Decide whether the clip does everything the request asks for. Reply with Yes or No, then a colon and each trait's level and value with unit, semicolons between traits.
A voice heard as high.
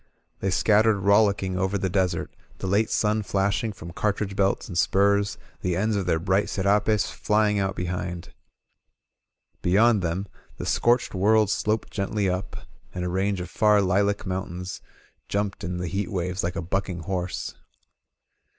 No: very low, 95 Hz